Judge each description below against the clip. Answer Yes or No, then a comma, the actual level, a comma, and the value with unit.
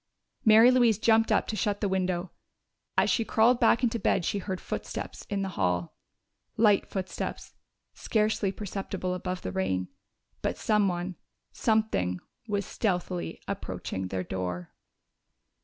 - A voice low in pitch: No, high, 195 Hz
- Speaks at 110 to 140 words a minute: Yes, slow, 135 wpm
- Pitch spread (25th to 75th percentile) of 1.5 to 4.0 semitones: No, average, 4.5 semitones